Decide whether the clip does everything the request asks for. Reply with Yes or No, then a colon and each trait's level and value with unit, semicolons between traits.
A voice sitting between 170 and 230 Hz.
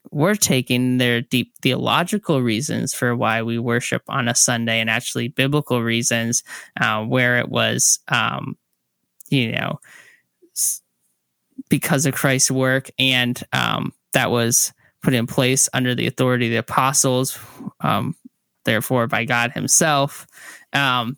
No: low, 125 Hz